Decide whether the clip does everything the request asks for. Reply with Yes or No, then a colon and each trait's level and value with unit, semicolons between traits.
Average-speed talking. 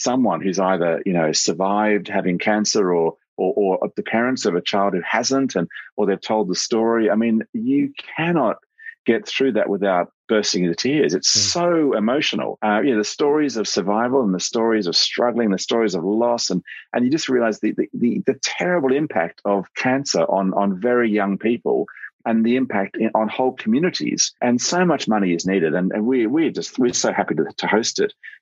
No: fast, 215 wpm